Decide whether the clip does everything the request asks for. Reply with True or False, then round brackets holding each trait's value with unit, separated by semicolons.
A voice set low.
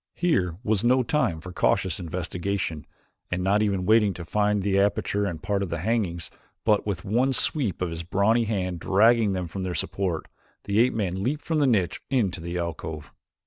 True (100 Hz)